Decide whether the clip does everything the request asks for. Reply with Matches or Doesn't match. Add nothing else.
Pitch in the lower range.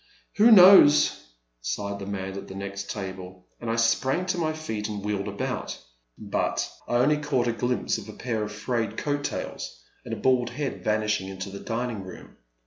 Matches